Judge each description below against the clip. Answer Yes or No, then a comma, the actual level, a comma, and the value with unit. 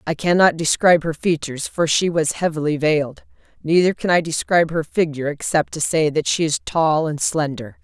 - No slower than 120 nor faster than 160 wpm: No, average, 190 wpm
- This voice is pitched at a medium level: Yes, medium, 160 Hz